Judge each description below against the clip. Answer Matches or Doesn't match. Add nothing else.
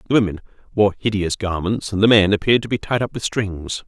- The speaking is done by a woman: Doesn't match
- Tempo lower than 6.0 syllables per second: Doesn't match